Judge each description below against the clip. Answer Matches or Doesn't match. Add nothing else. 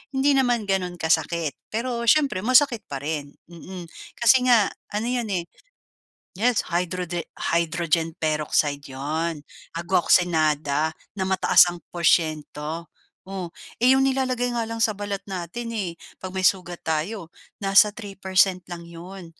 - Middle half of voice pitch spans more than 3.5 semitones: Matches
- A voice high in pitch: Doesn't match